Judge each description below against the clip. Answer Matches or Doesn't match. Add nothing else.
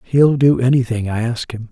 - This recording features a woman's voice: Doesn't match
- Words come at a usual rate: Doesn't match